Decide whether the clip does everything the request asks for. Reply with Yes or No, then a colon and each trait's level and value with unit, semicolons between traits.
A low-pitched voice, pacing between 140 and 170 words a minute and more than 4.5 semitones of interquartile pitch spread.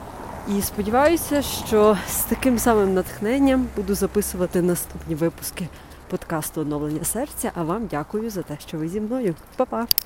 No: high, 205 Hz; average, 145 wpm; wide, 5.5 semitones